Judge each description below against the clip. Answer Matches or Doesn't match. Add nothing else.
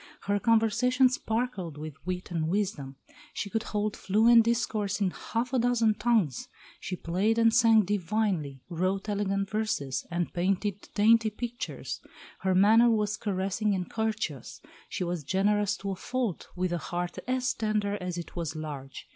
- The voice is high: Matches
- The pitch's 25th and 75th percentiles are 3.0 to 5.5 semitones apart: Matches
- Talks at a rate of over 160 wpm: Doesn't match